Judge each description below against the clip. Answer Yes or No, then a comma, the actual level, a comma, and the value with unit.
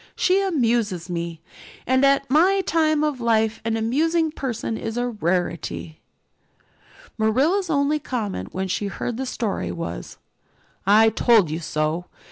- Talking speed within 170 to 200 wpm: No, slow, 135 wpm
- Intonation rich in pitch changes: Yes, wide, 7.1 semitones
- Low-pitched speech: No, high, 230 Hz